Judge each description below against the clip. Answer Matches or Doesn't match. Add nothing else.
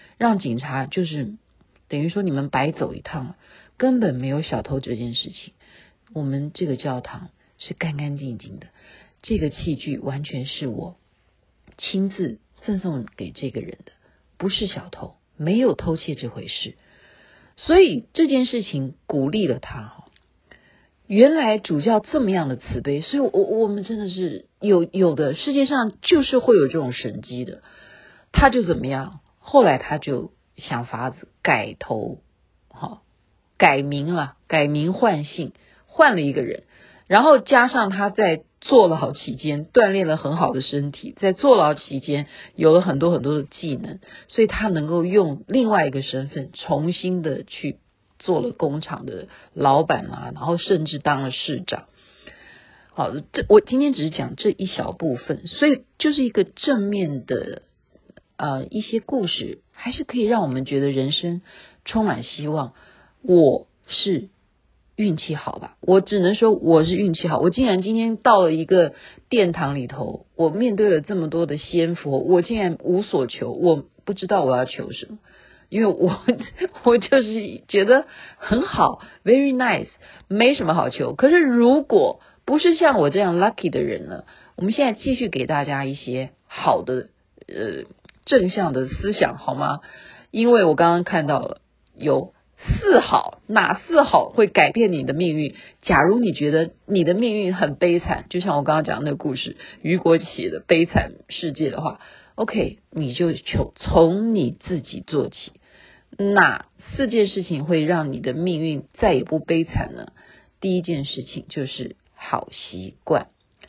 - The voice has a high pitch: Doesn't match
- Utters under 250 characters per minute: Matches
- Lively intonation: Matches